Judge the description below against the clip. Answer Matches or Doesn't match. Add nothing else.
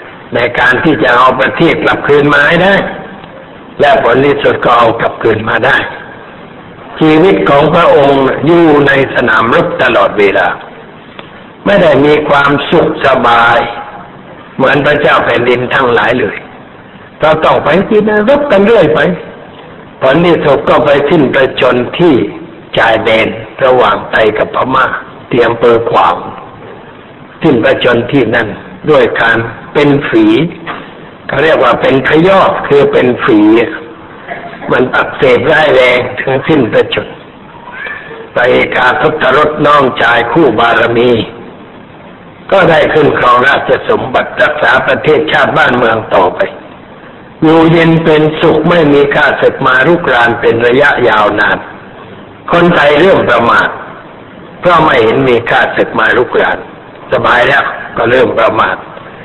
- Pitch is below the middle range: Doesn't match